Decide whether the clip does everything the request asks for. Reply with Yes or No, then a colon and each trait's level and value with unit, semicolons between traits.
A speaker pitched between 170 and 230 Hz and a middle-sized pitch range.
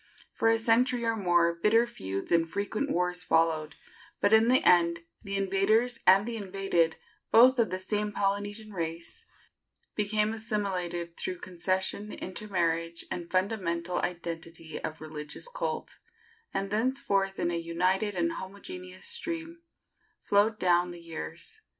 Yes: high, 190 Hz; average, 4.0 semitones